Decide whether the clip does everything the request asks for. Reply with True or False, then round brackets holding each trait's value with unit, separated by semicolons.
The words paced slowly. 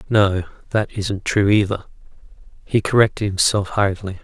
True (130 wpm)